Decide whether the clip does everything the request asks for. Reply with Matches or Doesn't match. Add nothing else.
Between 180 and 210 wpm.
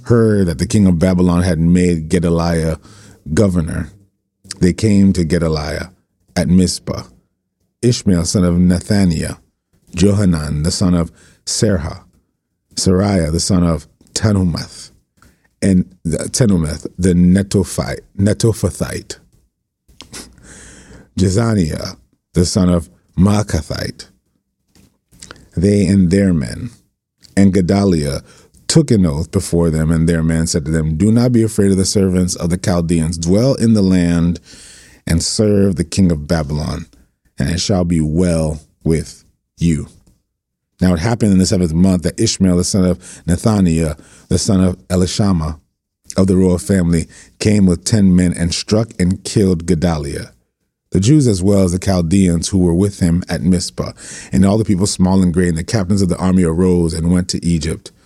Doesn't match